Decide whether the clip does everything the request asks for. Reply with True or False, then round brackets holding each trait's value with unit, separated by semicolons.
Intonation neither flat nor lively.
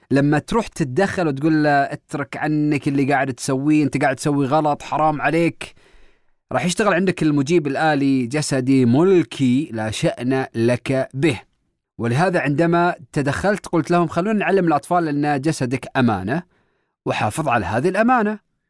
True (4.2 semitones)